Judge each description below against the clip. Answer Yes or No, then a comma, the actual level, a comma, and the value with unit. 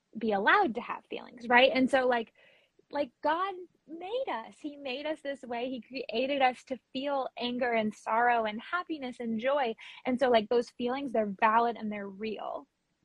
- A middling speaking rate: Yes, average, 185 wpm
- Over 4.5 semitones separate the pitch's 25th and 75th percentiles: No, average, 3.4 semitones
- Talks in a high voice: Yes, very high, 250 Hz